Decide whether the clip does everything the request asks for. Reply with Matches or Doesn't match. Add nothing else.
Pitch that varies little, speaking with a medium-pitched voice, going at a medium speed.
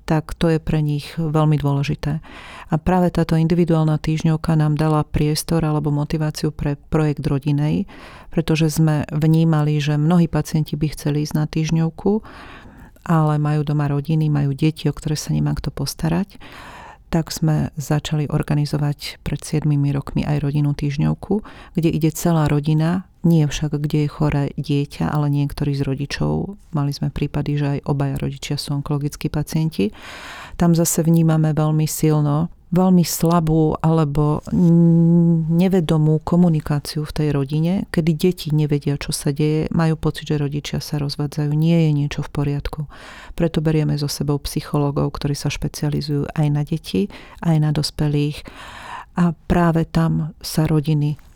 Matches